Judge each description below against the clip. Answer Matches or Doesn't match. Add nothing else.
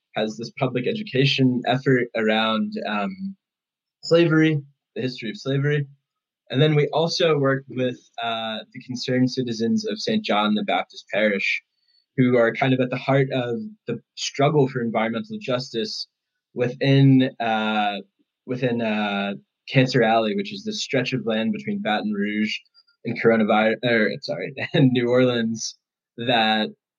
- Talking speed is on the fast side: Doesn't match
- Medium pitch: Doesn't match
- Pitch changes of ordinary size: Matches